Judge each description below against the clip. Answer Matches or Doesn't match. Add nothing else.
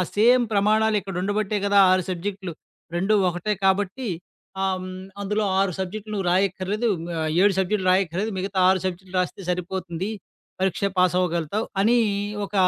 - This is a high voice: Matches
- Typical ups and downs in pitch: Doesn't match